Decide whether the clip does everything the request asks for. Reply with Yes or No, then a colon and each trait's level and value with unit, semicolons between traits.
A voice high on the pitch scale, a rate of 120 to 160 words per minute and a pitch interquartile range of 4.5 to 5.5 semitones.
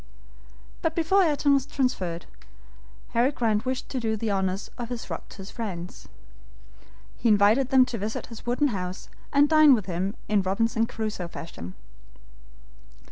Yes: high, 225 Hz; average, 155 wpm; average, 5.1 semitones